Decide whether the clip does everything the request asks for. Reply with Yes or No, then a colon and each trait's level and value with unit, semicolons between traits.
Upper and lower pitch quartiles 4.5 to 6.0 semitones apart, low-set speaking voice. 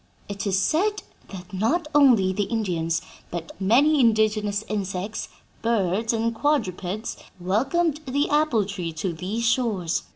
No: average, 5.1 semitones; high, 215 Hz